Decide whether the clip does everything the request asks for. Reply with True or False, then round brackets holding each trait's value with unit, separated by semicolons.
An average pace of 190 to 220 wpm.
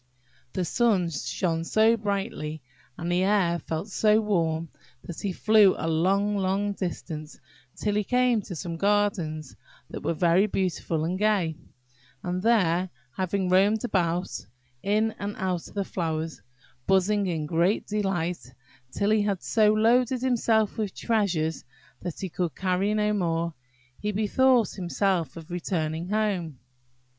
False (145 wpm)